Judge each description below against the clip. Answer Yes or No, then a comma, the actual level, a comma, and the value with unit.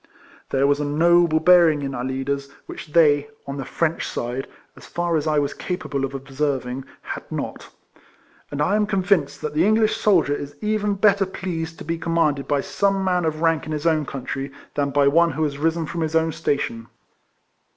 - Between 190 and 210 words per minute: Yes, average, 195 wpm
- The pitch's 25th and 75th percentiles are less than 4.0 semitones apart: Yes, average, 3.4 semitones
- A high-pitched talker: No, medium, 155 Hz